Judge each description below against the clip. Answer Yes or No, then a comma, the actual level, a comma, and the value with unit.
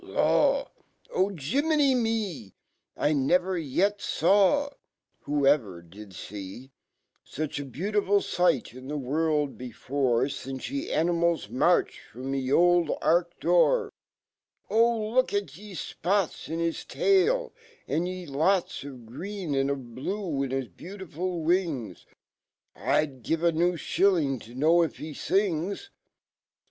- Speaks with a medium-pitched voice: Yes, medium, 165 Hz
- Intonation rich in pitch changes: Yes, wide, 6.3 semitones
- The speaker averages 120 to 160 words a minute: No, slow, 110 wpm